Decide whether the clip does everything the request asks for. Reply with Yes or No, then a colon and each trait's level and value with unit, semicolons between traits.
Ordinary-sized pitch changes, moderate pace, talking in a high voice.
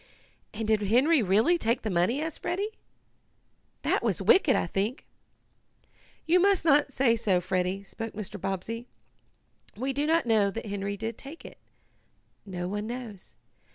No: wide, 5.7 semitones; average, 155 wpm; high, 225 Hz